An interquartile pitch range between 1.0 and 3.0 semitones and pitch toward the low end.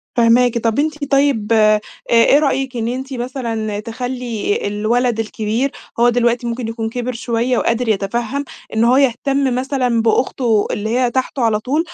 No: narrow, 2.5 semitones; high, 240 Hz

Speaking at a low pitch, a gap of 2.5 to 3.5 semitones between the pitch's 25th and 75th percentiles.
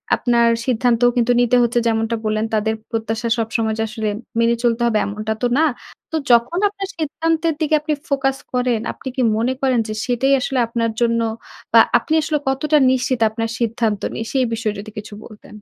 No: high, 235 Hz; average, 3.0 semitones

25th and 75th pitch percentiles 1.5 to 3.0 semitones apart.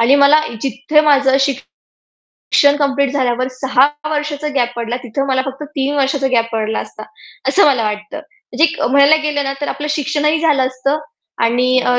Yes: narrow, 2.6 semitones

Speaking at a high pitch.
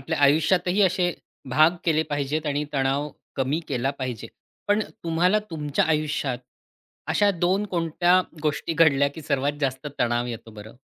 No: medium, 150 Hz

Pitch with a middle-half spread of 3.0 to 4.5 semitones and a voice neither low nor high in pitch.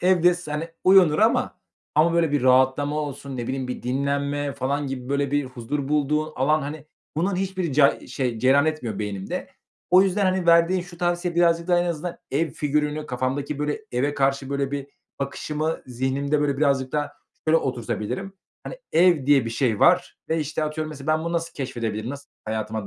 Yes: average, 3.8 semitones; medium, 145 Hz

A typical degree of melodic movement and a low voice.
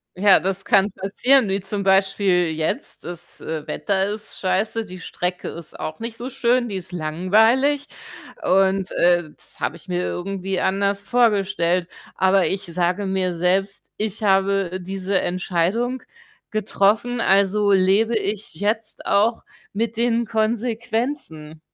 No: average, 3.1 semitones; high, 195 Hz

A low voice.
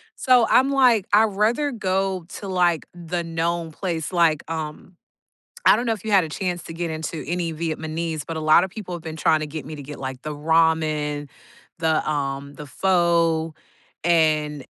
No: medium, 165 Hz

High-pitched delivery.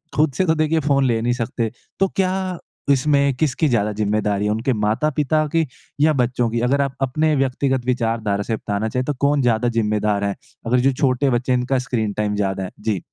No: low, 125 Hz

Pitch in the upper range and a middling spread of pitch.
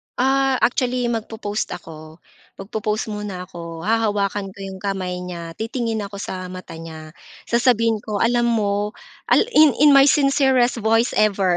Yes: high, 210 Hz; average, 4.2 semitones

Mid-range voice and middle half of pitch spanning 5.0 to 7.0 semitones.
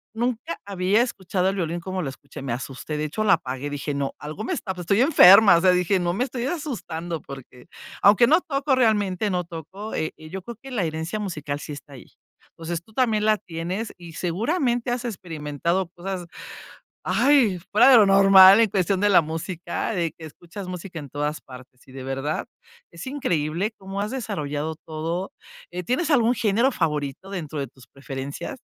Yes: medium, 180 Hz; wide, 5.5 semitones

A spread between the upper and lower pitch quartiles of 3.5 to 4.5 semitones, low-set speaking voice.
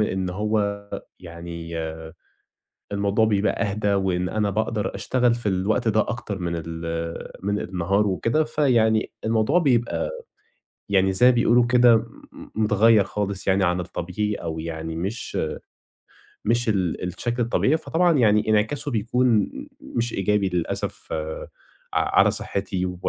Yes: average, 3.9 semitones; low, 105 Hz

